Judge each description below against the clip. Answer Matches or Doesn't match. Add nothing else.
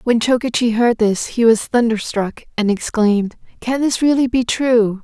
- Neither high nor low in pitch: Doesn't match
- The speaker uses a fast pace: Doesn't match